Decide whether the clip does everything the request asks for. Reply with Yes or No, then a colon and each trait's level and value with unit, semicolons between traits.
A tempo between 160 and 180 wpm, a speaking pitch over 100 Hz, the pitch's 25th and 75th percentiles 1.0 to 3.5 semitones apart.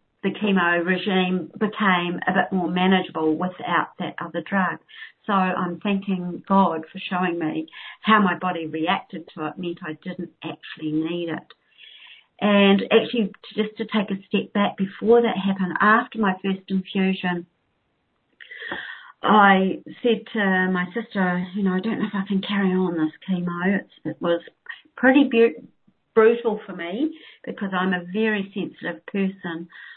No: average, 150 wpm; high, 190 Hz; average, 3.1 semitones